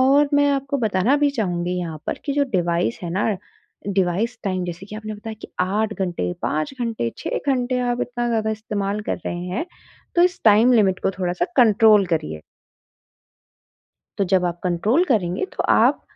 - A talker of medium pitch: No, high, 210 Hz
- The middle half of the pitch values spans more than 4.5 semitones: Yes, average, 5.2 semitones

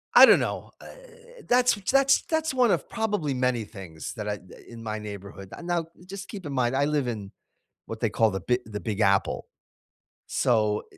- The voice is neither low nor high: No, low, 125 Hz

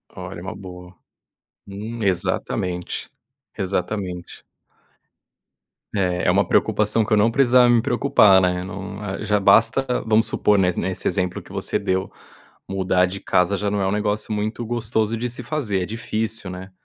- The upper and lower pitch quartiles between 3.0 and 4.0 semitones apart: Yes, average, 3.3 semitones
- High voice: No, low, 100 Hz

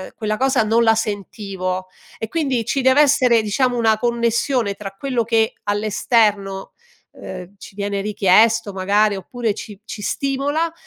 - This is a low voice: No, high, 220 Hz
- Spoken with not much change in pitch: No, average, 3.3 semitones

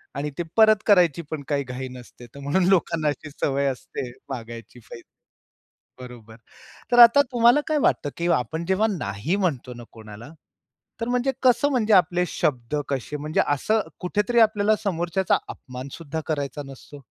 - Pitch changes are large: Yes, wide, 7.8 semitones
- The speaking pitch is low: No, medium, 155 Hz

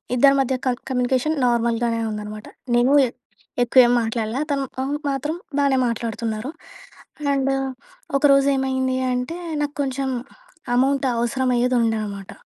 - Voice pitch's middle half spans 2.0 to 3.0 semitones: Yes, average, 2.7 semitones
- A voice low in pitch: No, very high, 255 Hz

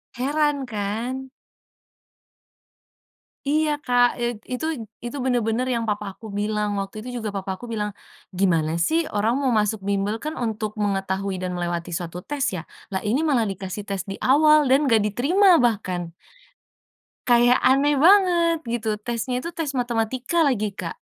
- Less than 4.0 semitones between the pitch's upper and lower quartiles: No, average, 5.0 semitones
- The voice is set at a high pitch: Yes, high, 235 Hz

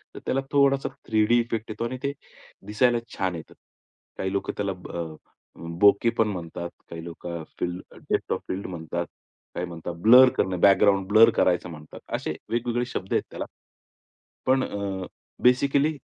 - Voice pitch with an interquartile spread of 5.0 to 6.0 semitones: Yes, average, 5.3 semitones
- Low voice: Yes, low, 100 Hz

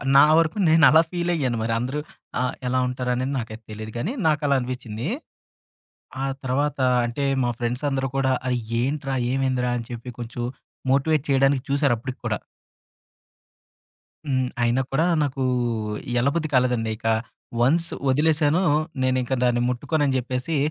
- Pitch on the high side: No, low, 130 Hz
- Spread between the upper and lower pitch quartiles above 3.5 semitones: No, average, 2.8 semitones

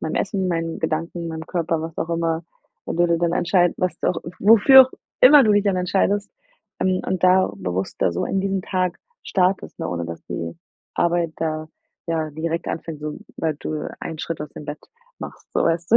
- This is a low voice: No, medium, 170 Hz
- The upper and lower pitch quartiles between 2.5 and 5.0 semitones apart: Yes, average, 2.8 semitones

